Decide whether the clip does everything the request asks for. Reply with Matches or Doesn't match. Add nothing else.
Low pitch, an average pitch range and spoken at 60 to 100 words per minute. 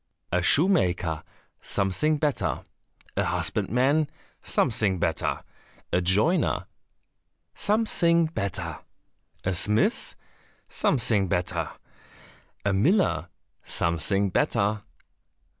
Doesn't match